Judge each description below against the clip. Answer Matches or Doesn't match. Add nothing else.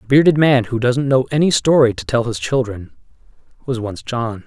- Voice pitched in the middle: Doesn't match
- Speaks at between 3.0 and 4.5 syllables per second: Doesn't match